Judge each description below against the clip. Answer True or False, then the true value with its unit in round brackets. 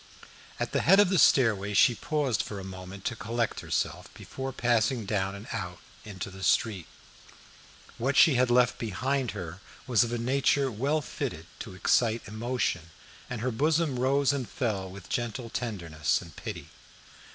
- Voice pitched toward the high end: False (115 Hz)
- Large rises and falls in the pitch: False (5.0 semitones)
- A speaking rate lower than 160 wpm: False (170 wpm)